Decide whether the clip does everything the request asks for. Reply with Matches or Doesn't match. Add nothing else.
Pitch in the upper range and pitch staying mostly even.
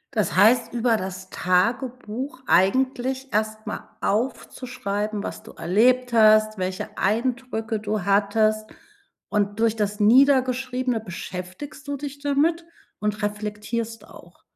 Doesn't match